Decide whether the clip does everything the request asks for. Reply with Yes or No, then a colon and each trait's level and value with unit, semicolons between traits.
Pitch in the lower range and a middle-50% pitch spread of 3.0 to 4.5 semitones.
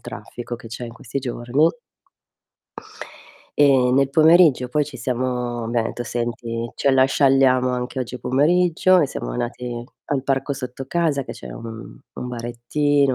No: low, 125 Hz; narrow, 2.6 semitones